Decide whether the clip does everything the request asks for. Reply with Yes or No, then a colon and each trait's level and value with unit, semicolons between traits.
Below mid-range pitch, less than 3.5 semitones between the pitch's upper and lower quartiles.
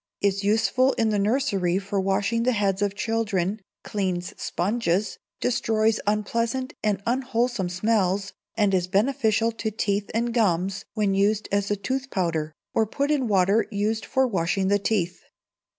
No: high, 205 Hz; average, 2.8 semitones